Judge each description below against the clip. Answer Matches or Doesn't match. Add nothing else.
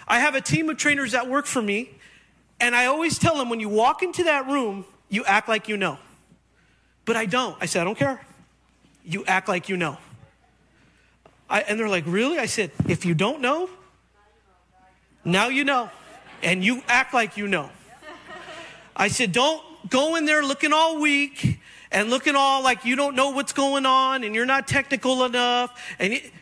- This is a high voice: Matches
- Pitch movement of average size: Doesn't match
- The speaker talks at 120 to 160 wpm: Doesn't match